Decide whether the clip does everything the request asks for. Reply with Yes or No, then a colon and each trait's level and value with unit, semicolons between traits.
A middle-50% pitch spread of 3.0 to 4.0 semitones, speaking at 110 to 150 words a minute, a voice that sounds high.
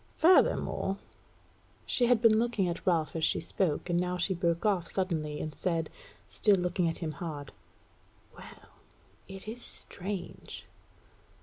No: average, 3.5 semitones; average, 145 wpm; medium, 180 Hz